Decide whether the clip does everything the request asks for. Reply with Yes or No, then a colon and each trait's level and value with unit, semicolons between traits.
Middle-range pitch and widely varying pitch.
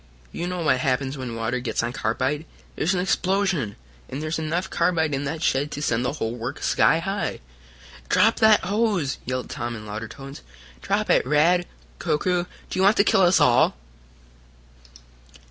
Yes: medium, 150 Hz; wide, 6.1 semitones